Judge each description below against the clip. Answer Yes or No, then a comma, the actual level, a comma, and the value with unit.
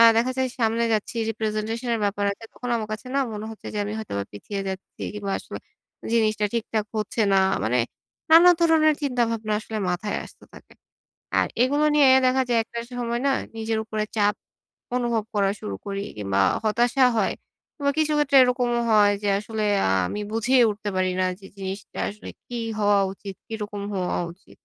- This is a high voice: Yes, high, 220 Hz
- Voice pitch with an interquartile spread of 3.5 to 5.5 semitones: No, average, 3.0 semitones